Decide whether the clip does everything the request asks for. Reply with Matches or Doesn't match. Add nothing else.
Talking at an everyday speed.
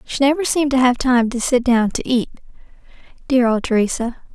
Matches